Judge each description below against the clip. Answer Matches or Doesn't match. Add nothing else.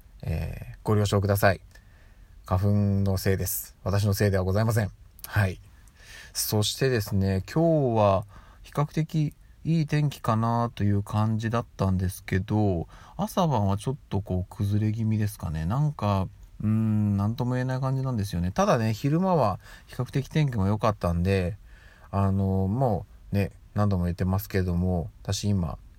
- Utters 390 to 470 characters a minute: Doesn't match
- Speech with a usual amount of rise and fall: Matches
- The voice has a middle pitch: Doesn't match